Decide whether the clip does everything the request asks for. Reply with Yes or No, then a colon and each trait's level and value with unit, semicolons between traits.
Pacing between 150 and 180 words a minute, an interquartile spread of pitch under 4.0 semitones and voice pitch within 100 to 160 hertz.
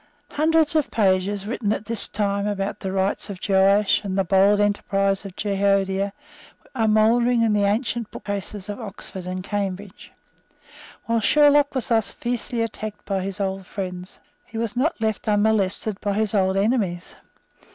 No: average, 160 wpm; narrow, 2.4 semitones; high, 205 Hz